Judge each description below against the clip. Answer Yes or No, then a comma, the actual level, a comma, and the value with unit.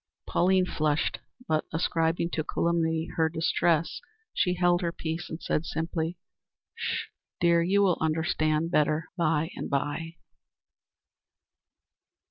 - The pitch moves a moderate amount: No, narrow, 1.3 semitones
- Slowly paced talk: Yes, slow, 115 wpm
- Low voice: No, medium, 165 Hz